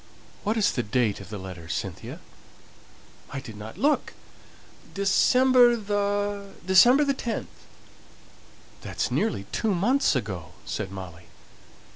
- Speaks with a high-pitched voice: Yes, high, 195 Hz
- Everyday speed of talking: No, slow, 115 wpm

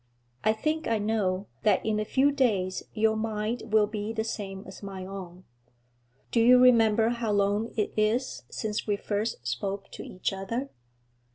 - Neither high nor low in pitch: No, high, 215 Hz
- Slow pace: No, average, 170 wpm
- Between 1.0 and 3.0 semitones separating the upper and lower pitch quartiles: Yes, narrow, 2.5 semitones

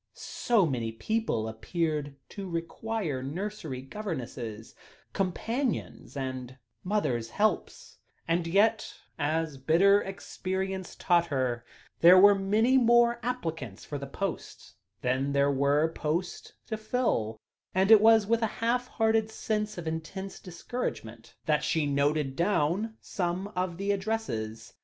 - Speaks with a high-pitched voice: No, medium, 175 Hz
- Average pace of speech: No, slow, 125 wpm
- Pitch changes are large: Yes, wide, 7.1 semitones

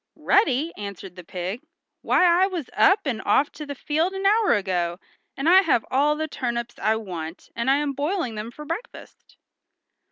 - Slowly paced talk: No, average, 180 wpm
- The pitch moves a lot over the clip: Yes, wide, 8.0 semitones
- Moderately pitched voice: No, very high, 275 Hz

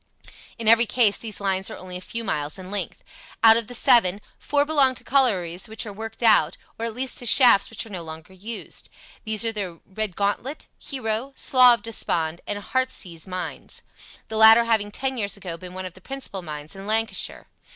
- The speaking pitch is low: No, high, 215 Hz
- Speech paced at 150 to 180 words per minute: No, average, 200 wpm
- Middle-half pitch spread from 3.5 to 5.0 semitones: Yes, average, 3.9 semitones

